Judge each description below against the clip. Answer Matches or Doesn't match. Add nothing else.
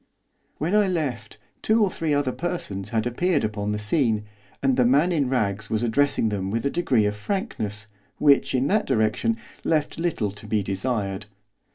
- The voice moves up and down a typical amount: Doesn't match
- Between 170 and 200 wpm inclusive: Matches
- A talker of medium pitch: Doesn't match